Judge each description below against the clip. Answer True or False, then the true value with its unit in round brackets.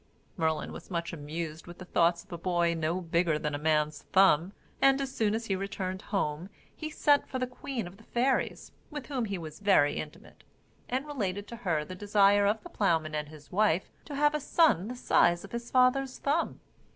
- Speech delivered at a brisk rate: True (210 wpm)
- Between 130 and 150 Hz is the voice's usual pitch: False (195 Hz)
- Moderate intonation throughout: False (6.7 semitones)